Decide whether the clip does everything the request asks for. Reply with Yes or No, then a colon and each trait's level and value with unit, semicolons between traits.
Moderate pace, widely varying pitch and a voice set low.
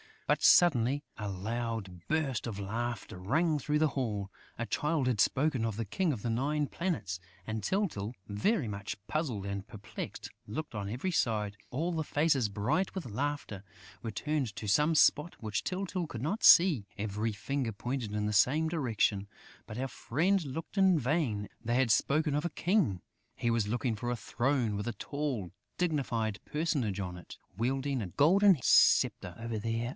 Yes: average, 175 wpm; wide, 6.3 semitones; low, 120 Hz